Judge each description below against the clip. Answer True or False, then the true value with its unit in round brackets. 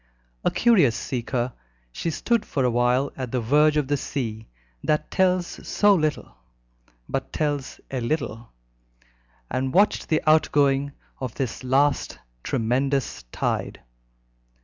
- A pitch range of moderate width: True (3.6 semitones)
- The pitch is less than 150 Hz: True (140 Hz)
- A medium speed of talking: False (125 wpm)